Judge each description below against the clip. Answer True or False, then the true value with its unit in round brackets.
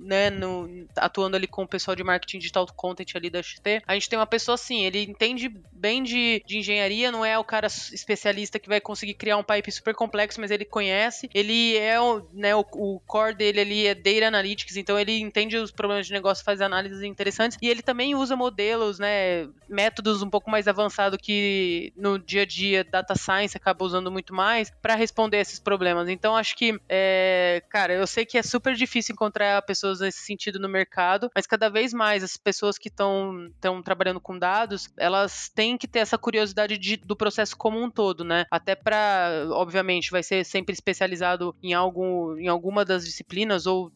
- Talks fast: True (200 wpm)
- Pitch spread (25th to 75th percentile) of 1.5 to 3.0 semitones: True (2.5 semitones)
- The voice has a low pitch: False (205 Hz)